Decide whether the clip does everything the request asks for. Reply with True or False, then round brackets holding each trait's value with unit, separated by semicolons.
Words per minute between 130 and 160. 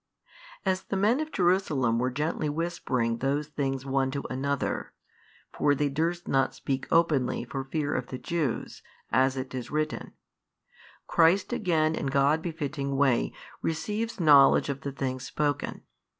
True (150 wpm)